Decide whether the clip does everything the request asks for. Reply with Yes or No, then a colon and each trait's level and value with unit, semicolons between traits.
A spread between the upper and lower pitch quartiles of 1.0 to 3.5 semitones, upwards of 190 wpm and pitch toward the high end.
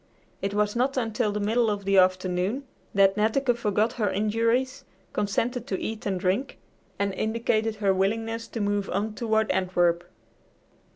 No: average, 2.7 semitones; average, 155 wpm; high, 210 Hz